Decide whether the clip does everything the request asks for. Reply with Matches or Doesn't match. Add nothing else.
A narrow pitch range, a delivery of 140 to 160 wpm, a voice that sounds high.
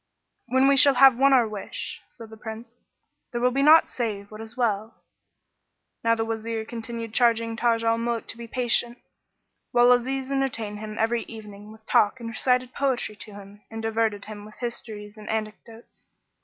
Doesn't match